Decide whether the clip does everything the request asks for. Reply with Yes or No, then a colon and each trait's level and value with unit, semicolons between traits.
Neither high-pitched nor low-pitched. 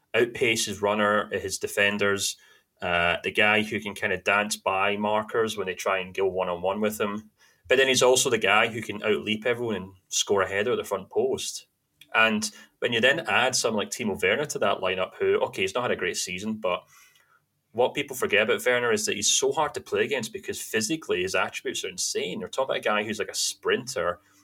No: low, 110 Hz